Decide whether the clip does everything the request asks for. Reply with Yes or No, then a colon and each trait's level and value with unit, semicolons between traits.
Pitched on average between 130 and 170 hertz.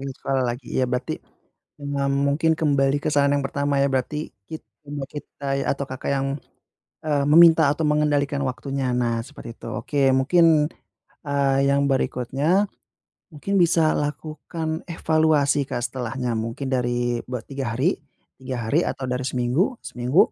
Yes: medium, 140 Hz